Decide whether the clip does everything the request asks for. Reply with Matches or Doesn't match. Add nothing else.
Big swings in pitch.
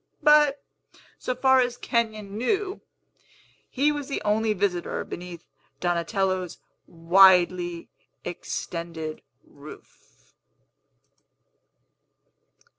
Matches